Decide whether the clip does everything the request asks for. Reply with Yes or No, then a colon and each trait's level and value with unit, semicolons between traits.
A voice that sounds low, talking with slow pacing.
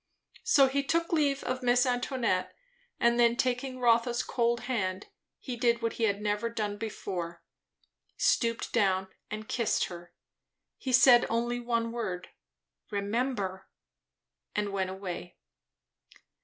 No: high, 235 Hz; slow, 130 wpm